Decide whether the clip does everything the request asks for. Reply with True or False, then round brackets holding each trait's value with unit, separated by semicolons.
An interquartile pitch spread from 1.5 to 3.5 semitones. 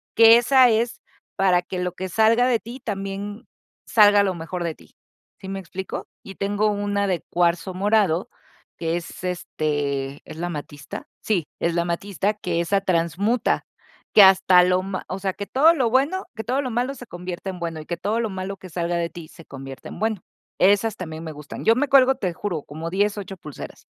False (4.0 semitones)